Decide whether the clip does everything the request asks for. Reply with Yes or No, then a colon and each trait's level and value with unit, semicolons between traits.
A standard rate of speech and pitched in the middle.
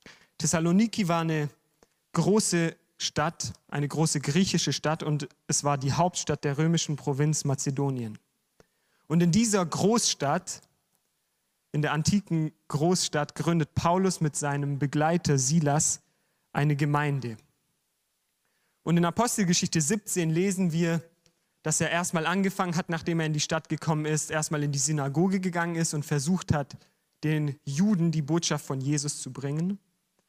Yes: average, 135 wpm; medium, 160 Hz